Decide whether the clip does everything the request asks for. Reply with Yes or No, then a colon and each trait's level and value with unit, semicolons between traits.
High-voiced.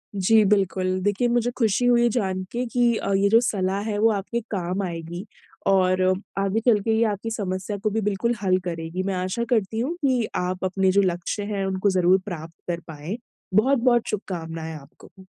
Yes: high, 195 Hz